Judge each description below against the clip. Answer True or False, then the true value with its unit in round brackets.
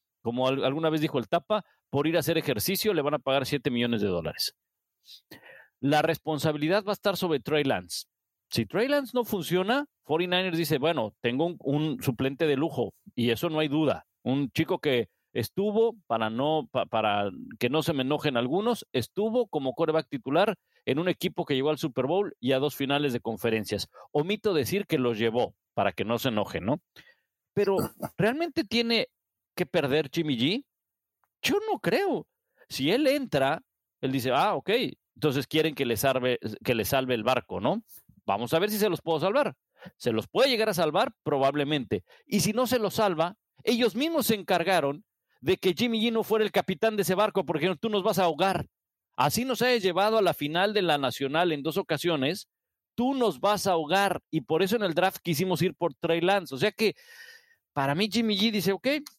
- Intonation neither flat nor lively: False (7.1 semitones)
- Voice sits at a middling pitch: True (165 Hz)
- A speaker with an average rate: False (200 wpm)